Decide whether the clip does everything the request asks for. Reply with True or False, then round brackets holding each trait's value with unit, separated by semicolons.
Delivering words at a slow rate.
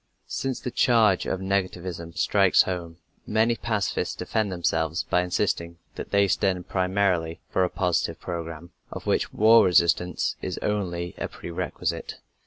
False (145 wpm)